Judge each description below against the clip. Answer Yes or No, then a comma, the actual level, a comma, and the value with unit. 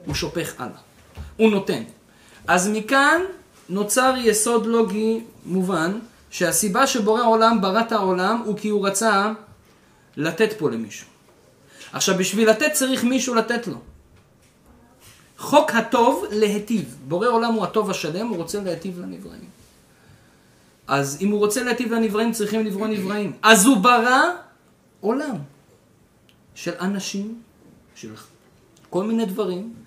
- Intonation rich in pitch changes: No, average, 3.5 semitones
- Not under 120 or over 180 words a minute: Yes, average, 125 wpm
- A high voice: Yes, high, 215 Hz